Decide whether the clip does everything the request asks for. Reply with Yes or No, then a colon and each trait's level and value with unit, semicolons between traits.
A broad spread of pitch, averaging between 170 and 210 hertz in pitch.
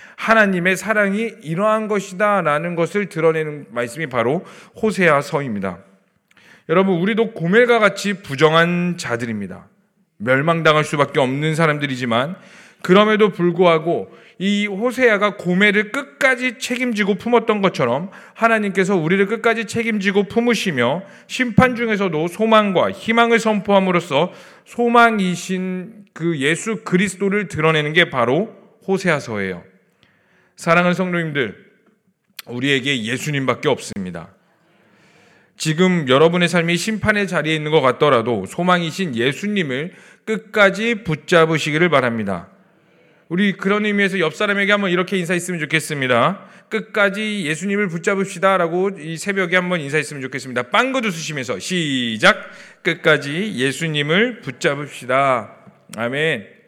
No: average, 5.0 semitones; medium, 185 Hz